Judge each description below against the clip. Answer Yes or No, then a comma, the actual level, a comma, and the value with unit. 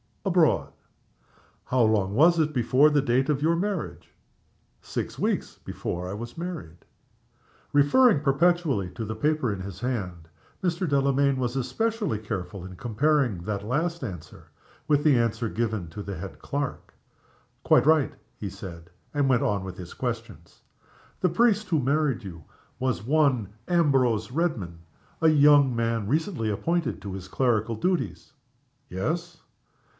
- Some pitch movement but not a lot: No, wide, 7.0 semitones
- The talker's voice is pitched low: Yes, low, 130 Hz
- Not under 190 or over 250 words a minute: No, average, 145 wpm